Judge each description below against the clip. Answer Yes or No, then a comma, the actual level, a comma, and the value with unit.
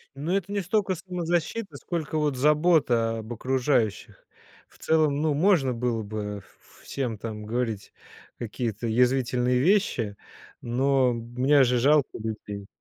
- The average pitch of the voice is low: Yes, low, 130 Hz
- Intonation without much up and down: No, average, 5.2 semitones